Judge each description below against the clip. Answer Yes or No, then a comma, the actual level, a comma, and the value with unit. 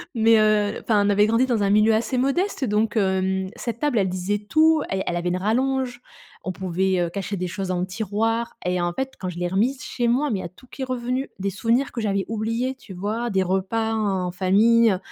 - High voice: Yes, high, 210 Hz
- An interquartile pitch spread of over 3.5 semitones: Yes, average, 3.9 semitones